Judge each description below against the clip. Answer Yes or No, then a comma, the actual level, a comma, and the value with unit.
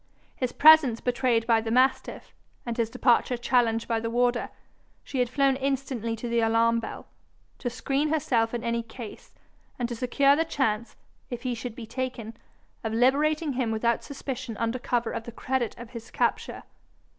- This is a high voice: Yes, high, 240 Hz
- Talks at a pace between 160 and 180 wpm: Yes, average, 175 wpm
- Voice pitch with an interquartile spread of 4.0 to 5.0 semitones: No, narrow, 2.4 semitones